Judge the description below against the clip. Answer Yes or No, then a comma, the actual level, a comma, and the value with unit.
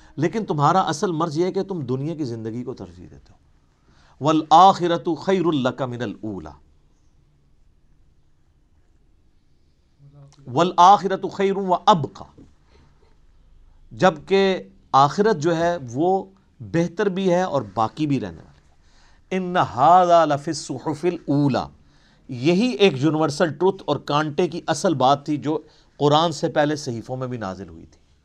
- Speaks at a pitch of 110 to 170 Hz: Yes, medium, 140 Hz